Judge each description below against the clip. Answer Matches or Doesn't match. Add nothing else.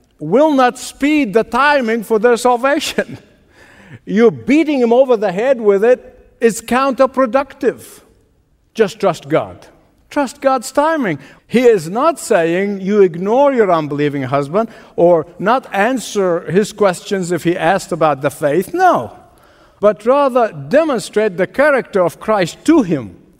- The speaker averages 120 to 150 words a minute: Matches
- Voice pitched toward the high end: Matches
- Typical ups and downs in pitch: Doesn't match